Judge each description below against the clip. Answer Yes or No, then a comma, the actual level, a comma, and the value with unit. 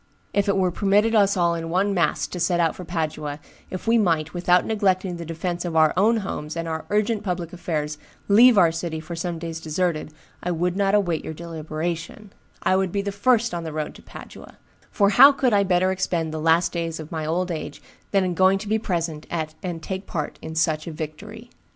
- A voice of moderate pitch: Yes, medium, 175 Hz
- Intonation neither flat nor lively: Yes, average, 3.4 semitones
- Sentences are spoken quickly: Yes, fast, 220 wpm